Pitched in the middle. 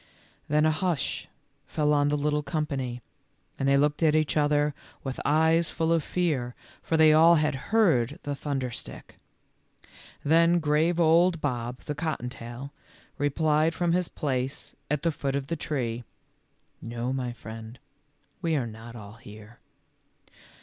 Yes: medium, 145 Hz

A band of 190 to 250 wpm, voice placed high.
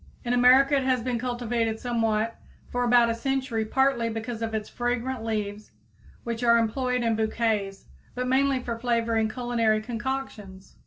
No: average, 155 wpm; high, 235 Hz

